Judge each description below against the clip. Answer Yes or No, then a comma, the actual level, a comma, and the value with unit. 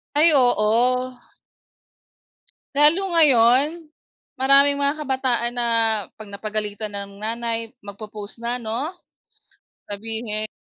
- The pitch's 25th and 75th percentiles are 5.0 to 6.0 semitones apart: No, average, 4.3 semitones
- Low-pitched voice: No, high, 235 Hz